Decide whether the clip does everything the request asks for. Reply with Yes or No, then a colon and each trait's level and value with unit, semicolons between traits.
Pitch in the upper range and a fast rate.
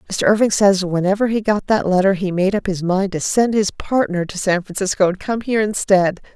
Yes: high, 195 Hz; fast, 225 wpm